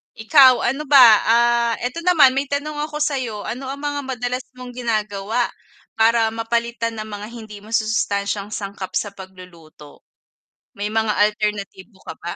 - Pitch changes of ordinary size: Yes, average, 3.7 semitones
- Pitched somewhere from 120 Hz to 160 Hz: No, high, 225 Hz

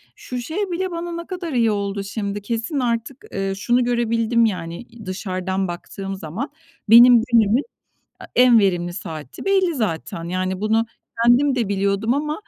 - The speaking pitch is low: No, high, 225 Hz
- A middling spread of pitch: Yes, average, 4.4 semitones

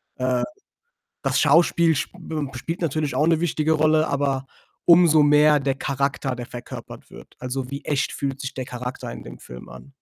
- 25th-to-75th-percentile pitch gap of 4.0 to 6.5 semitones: No, average, 2.8 semitones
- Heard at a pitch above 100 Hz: Yes, medium, 140 Hz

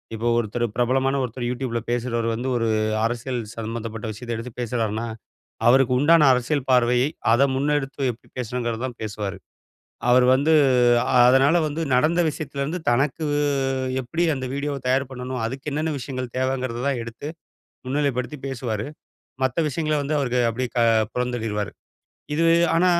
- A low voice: Yes, low, 125 Hz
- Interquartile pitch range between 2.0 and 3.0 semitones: Yes, average, 2.7 semitones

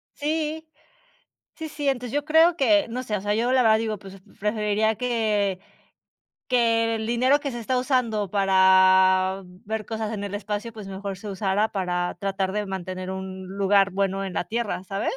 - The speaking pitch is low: No, high, 210 Hz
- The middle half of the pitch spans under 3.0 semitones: No, average, 3.7 semitones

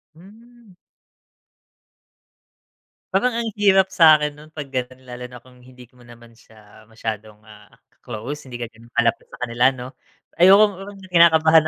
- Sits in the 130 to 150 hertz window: Yes, low, 135 Hz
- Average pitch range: No, wide, 7.7 semitones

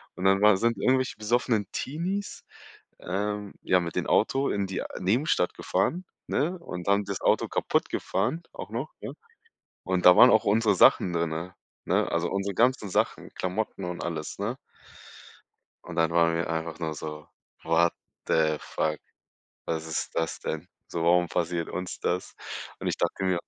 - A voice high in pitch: No, very low, 90 Hz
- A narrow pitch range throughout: No, average, 4.1 semitones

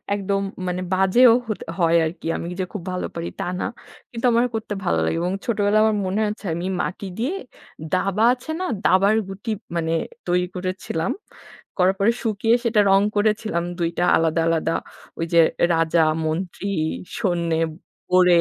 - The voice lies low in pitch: No, high, 190 Hz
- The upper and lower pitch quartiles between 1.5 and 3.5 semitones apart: No, average, 3.9 semitones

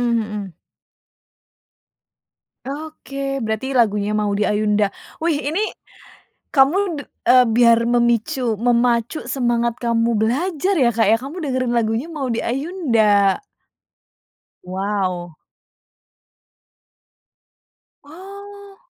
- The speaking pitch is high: Yes, high, 235 Hz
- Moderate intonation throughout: Yes, average, 4.2 semitones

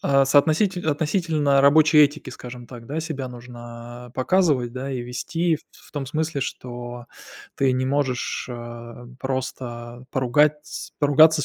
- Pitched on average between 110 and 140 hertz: Yes, low, 135 Hz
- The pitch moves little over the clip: No, average, 3.7 semitones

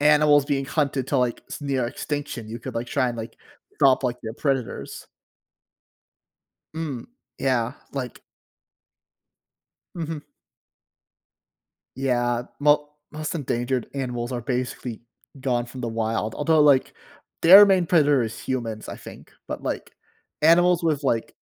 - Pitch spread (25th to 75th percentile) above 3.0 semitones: Yes, average, 3.5 semitones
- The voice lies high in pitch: No, low, 135 Hz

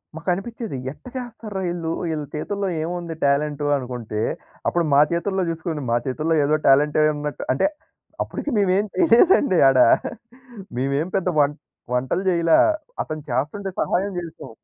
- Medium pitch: Yes, medium, 165 Hz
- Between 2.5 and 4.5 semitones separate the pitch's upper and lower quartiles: No, average, 5.0 semitones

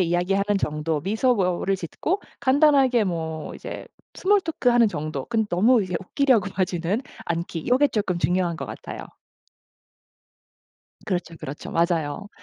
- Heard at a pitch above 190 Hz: No, medium, 185 Hz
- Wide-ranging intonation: Yes, wide, 6.0 semitones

